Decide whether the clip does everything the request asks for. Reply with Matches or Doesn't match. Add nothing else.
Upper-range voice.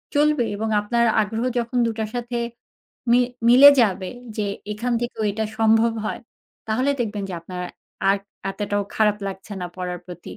Matches